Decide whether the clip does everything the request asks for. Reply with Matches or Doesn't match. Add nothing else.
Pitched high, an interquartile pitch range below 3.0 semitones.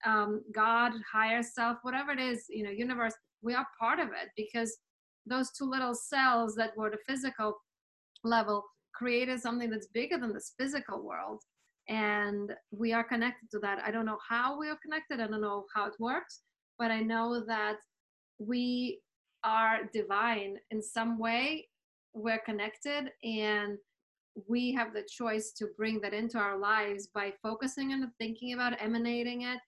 Matches